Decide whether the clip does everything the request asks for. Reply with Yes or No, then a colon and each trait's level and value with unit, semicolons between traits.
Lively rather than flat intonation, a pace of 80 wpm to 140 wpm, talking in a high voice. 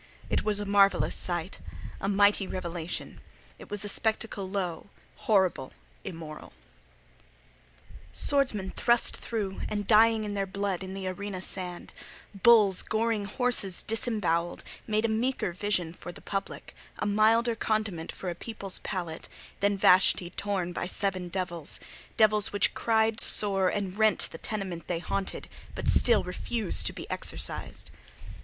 No: average, 2.9 semitones; slow, 135 wpm; high, 200 Hz